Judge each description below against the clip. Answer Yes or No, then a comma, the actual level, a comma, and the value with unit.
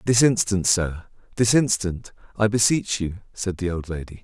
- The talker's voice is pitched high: No, low, 100 Hz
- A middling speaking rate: Yes, average, 155 wpm